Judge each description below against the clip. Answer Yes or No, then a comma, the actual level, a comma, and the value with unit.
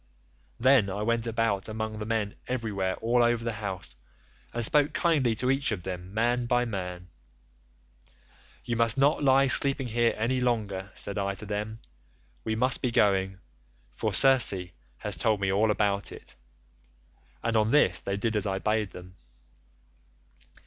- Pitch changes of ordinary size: Yes, average, 3.5 semitones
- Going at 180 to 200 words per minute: No, average, 160 wpm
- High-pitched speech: No, low, 110 Hz